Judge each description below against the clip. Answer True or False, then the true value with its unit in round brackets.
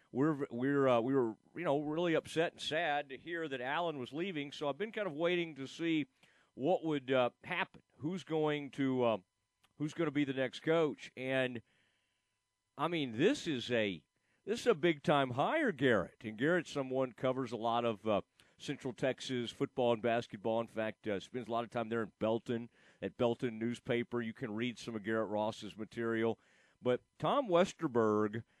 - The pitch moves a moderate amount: True (4.7 semitones)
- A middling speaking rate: True (190 wpm)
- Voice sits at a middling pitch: False (130 Hz)